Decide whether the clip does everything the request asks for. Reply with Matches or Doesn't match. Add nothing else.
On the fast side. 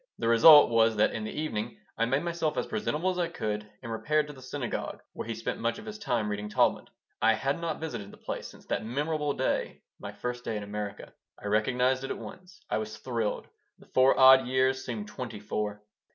Matches